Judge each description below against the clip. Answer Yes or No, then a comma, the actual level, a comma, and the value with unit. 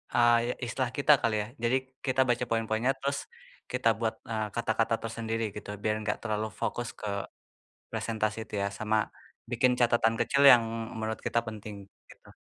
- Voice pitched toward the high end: No, low, 115 Hz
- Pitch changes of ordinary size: No, narrow, 1.8 semitones